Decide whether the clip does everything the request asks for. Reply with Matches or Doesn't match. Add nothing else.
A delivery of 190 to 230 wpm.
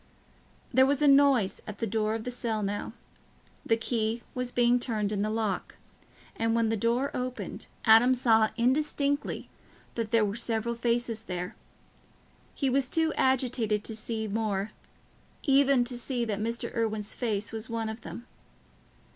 Doesn't match